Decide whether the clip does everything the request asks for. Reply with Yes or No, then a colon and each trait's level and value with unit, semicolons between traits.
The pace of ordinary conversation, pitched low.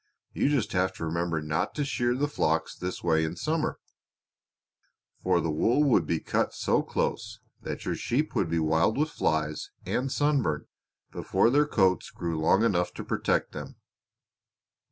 Yes: average, 160 wpm; very low, 90 Hz